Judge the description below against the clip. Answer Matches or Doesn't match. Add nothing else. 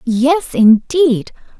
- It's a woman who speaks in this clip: Matches